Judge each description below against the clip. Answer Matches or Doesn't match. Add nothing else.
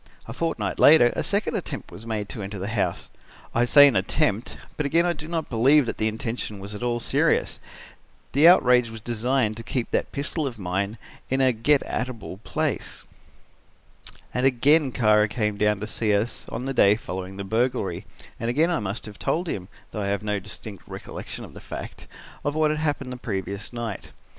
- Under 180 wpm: Doesn't match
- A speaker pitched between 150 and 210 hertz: Doesn't match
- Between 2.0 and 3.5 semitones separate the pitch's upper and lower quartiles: Doesn't match